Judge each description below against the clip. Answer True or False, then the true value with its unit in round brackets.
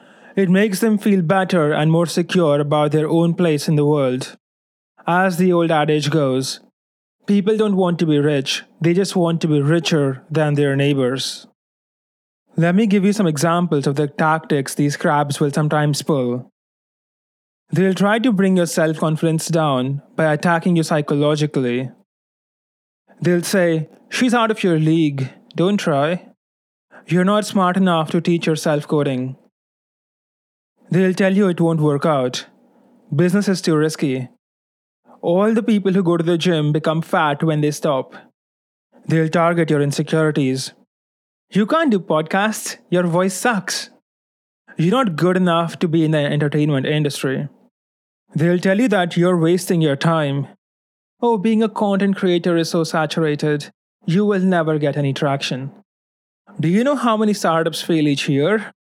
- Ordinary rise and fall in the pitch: True (4.0 semitones)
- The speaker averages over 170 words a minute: False (155 wpm)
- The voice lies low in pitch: False (165 Hz)